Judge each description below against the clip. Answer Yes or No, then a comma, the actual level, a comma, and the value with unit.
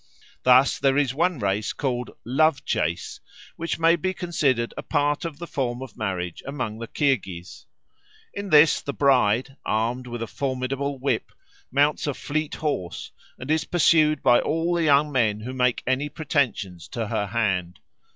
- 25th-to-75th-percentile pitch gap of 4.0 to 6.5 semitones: Yes, average, 4.4 semitones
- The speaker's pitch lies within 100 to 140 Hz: Yes, low, 135 Hz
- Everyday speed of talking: Yes, average, 170 wpm